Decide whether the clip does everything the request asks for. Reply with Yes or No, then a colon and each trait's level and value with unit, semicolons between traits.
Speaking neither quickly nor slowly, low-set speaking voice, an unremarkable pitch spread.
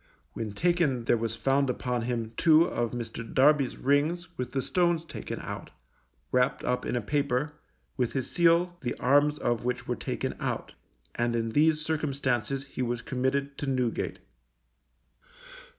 Yes: average, 155 wpm; low, 130 Hz; average, 3.7 semitones